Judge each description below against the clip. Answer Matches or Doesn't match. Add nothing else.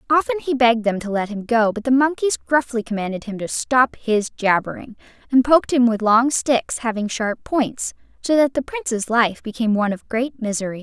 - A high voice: Matches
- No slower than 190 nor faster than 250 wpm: Matches